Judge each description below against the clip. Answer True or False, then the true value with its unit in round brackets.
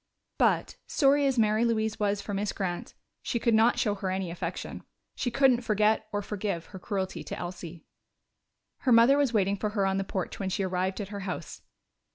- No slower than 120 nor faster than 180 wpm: False (200 wpm)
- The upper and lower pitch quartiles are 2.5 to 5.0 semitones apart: True (3.2 semitones)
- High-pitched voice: True (205 Hz)